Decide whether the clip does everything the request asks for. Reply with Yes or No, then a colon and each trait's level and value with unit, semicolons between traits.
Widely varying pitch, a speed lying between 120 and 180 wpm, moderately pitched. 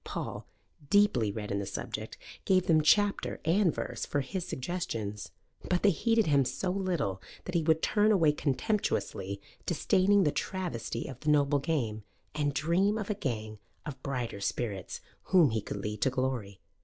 Yes: wide, 8.6 semitones; average, 170 wpm; medium, 145 Hz